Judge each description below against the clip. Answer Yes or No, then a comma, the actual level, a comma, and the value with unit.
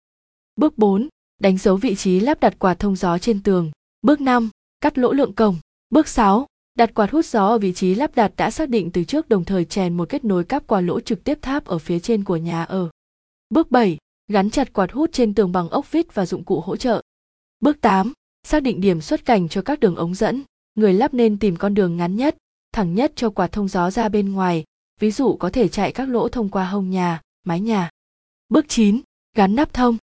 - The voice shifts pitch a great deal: No, average, 4.8 semitones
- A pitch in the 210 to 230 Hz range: Yes, high, 215 Hz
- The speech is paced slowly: No, average, 230 wpm